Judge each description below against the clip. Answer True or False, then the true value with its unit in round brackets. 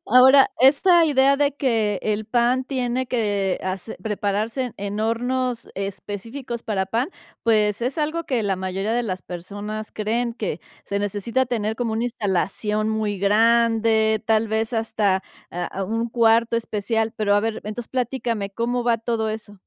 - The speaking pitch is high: True (225 Hz)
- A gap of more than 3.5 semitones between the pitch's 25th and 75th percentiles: False (2.8 semitones)